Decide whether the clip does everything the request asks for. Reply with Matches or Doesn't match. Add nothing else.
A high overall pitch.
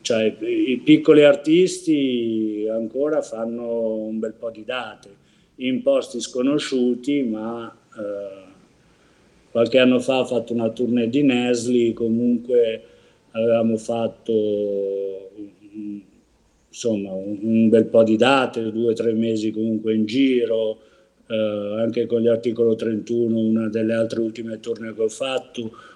Doesn't match